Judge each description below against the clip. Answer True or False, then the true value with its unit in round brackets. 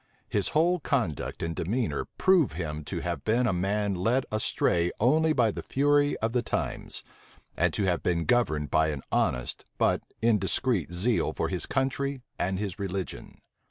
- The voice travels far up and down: True (6.7 semitones)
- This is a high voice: False (105 Hz)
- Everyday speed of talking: True (165 wpm)